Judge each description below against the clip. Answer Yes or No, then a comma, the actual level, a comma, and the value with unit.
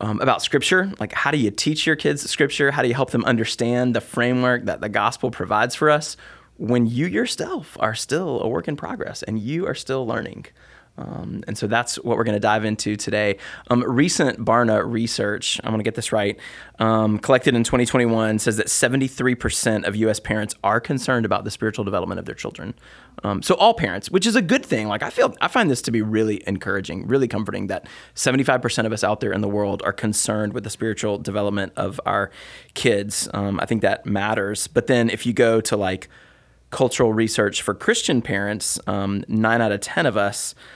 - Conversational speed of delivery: No, fast, 210 wpm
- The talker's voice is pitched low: Yes, low, 110 Hz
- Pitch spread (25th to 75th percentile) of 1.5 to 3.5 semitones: Yes, average, 3.1 semitones